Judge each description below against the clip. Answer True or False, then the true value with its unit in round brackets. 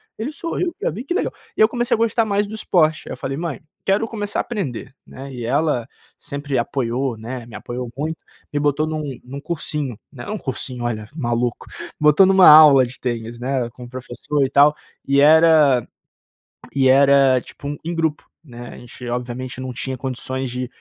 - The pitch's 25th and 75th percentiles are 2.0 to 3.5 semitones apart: False (4.2 semitones)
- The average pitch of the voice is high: False (140 Hz)